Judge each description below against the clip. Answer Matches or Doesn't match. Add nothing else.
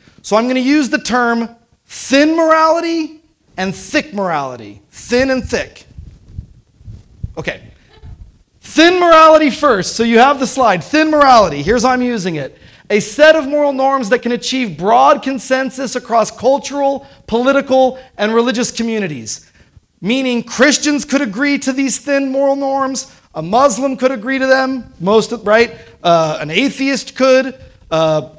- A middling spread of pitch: Matches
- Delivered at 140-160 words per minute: Matches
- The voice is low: Doesn't match